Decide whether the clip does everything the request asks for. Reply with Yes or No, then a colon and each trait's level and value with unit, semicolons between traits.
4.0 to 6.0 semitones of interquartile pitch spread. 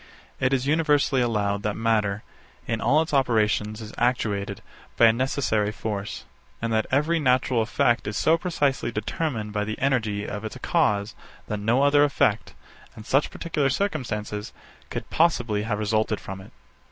Yes: average, 4.6 semitones